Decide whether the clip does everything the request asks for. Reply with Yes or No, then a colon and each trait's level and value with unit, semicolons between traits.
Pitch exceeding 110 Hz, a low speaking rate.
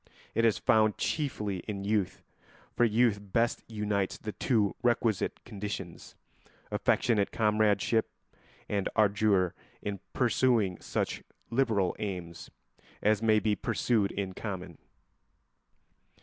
No: low, 105 Hz; slow, 105 wpm